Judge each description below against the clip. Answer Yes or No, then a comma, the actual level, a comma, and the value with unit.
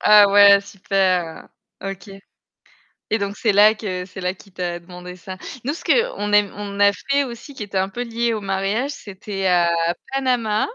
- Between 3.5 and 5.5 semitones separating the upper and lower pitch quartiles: No, average, 2.7 semitones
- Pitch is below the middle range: No, high, 200 Hz